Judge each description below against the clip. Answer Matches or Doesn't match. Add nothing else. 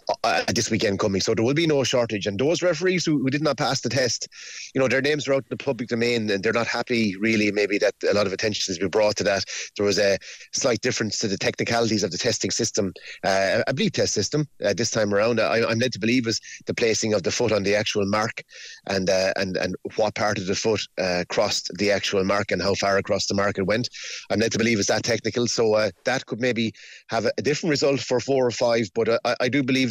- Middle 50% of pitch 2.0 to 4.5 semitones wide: Matches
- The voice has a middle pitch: Doesn't match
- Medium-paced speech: Doesn't match